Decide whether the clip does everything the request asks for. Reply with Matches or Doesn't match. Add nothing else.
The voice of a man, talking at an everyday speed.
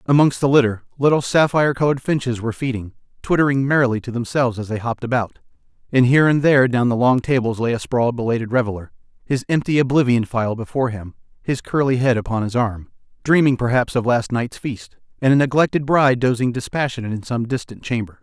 Matches